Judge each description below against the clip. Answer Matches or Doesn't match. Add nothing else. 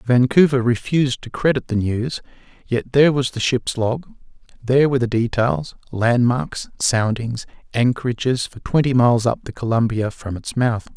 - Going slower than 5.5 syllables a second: Matches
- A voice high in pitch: Doesn't match